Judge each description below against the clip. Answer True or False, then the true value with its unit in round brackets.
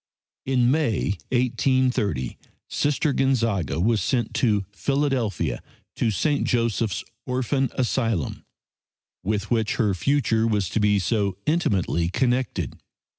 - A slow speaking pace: True (110 wpm)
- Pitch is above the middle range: False (115 Hz)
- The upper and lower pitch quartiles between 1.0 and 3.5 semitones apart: False (4.3 semitones)